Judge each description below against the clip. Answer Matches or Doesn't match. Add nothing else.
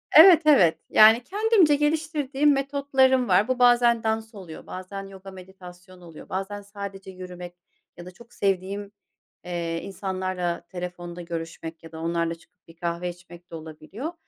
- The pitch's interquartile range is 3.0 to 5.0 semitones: Doesn't match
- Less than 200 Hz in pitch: Matches